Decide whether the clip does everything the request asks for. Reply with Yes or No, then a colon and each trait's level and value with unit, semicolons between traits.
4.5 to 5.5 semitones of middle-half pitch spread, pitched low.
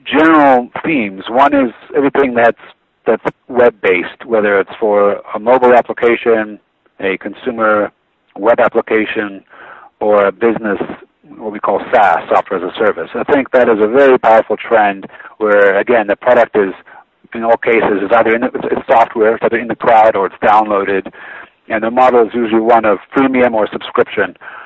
No: average, 2.9 semitones; low, 115 Hz